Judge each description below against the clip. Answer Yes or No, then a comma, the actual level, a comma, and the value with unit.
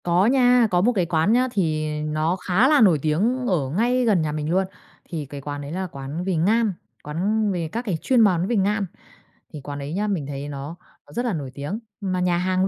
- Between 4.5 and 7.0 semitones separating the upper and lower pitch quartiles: Yes, wide, 5.6 semitones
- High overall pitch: No, medium, 180 Hz